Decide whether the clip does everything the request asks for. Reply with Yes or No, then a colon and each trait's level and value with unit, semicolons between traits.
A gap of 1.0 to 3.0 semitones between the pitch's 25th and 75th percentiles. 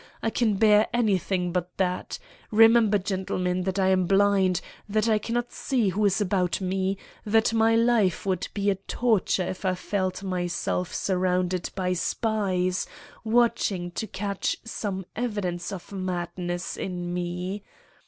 Yes: average, 2.7 semitones